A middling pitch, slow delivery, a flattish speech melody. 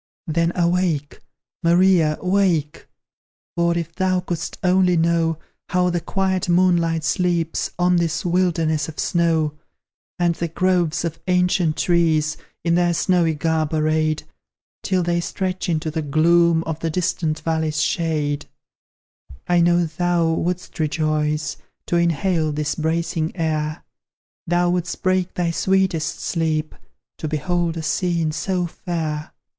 Yes: medium, 170 Hz; slow, 130 wpm; narrow, 2.0 semitones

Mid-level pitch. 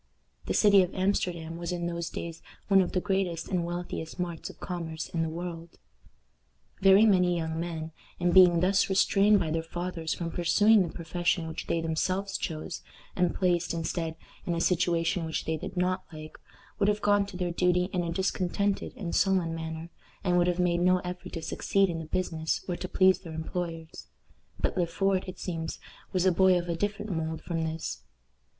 Yes: medium, 175 Hz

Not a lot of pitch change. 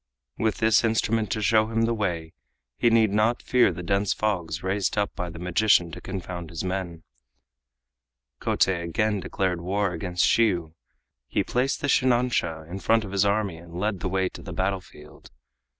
No: average, 3.8 semitones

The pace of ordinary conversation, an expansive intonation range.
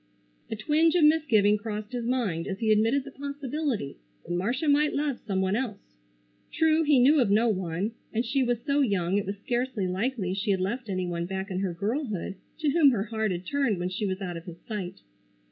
No: fast, 215 wpm; wide, 6.0 semitones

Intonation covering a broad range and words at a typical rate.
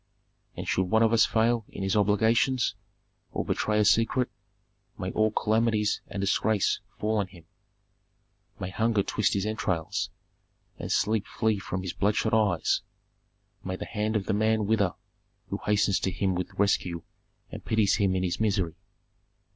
No: average, 2.7 semitones; average, 160 wpm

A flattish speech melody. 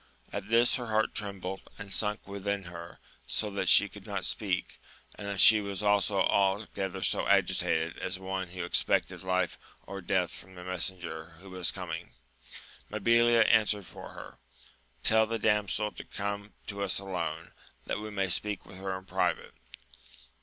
Yes: narrow, 2.2 semitones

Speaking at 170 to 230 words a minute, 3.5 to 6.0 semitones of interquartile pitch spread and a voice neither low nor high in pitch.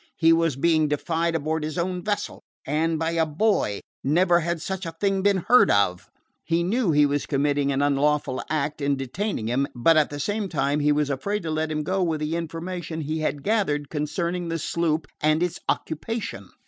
No: average, 200 wpm; average, 3.0 semitones; medium, 160 Hz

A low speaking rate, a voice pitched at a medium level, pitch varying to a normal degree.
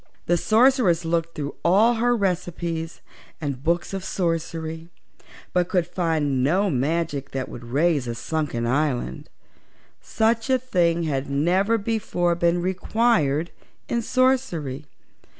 Yes: slow, 125 wpm; medium, 170 Hz; average, 4.8 semitones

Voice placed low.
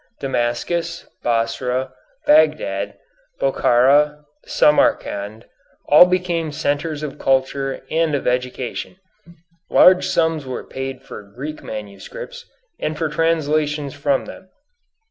No: medium, 145 Hz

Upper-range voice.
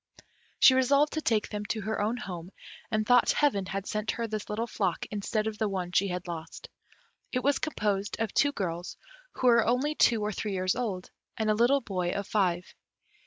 Yes: high, 215 Hz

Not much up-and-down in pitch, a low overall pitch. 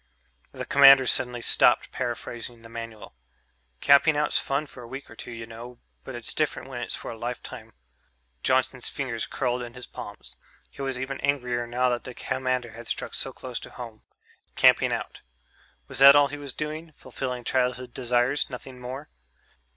Yes: narrow, 2.1 semitones; low, 125 Hz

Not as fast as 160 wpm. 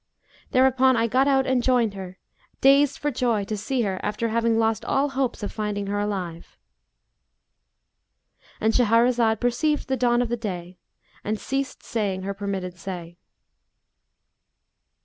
Yes: average, 140 wpm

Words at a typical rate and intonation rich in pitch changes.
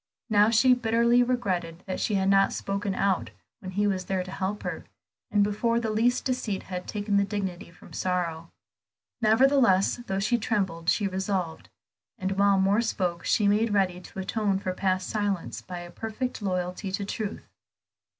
No: average, 175 wpm; narrow, 2.6 semitones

